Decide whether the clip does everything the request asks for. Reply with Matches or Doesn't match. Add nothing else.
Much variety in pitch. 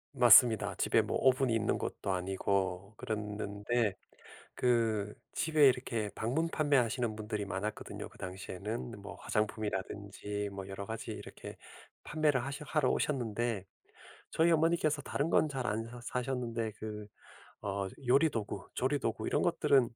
Doesn't match